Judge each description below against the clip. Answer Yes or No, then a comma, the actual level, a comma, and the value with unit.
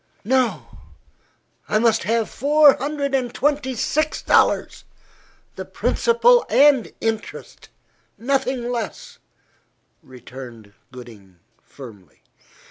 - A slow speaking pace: Yes, slow, 90 wpm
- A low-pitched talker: No, high, 240 Hz